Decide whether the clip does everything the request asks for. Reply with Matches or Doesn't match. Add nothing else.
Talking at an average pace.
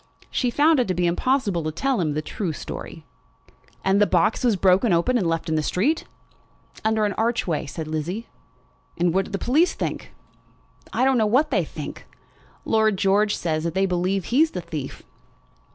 Matches